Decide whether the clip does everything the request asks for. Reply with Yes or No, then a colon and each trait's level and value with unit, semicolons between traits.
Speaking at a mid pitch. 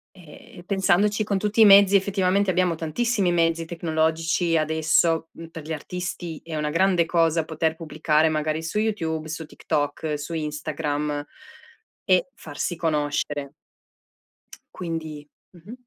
Yes: medium, 165 Hz